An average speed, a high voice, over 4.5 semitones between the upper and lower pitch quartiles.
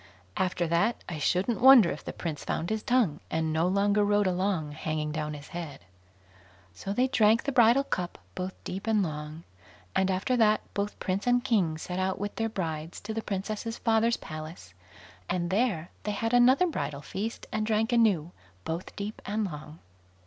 Yes: average, 180 wpm; high, 195 Hz; wide, 5.5 semitones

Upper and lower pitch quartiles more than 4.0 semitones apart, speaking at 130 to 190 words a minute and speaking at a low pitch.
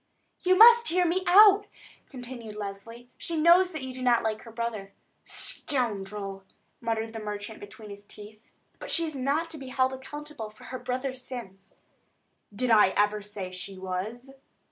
No: average, 5.1 semitones; average, 170 wpm; high, 235 Hz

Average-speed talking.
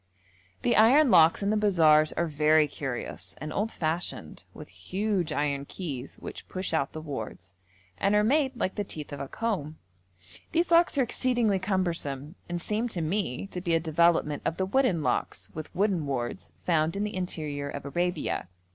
Yes: average, 180 wpm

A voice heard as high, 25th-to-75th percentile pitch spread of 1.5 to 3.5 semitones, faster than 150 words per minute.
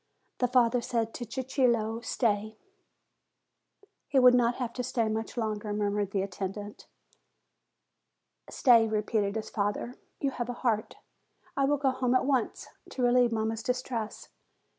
No: high, 230 Hz; average, 2.7 semitones; average, 140 wpm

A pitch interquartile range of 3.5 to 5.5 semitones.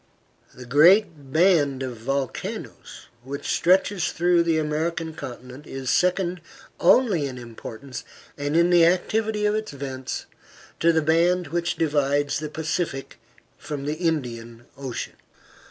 Yes: average, 4.3 semitones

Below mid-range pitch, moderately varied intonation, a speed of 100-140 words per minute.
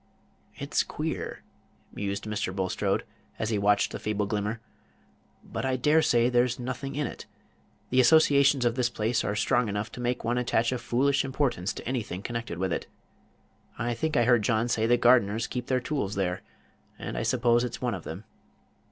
No: low, 120 Hz; average, 3.4 semitones; average, 185 wpm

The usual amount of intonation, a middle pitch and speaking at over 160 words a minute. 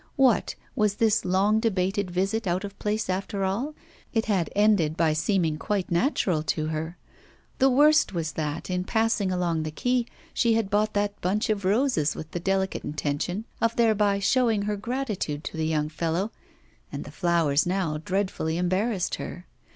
No: average, 4.3 semitones; high, 195 Hz; average, 170 wpm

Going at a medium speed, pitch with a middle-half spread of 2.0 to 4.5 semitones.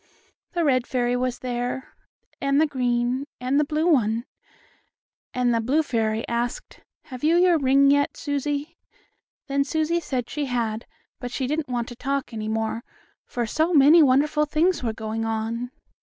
Yes: average, 165 wpm; average, 3.7 semitones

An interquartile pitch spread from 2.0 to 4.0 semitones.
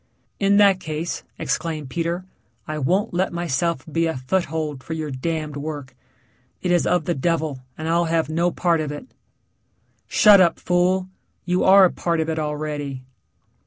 Yes: narrow, 2.6 semitones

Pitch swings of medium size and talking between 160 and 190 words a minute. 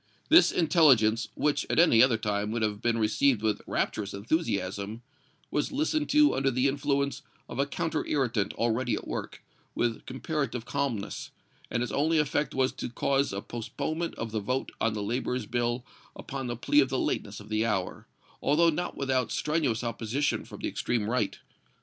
Yes: average, 4.3 semitones; average, 175 wpm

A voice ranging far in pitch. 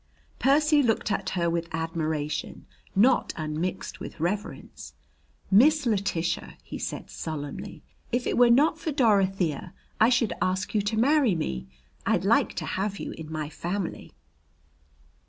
Yes: wide, 6.6 semitones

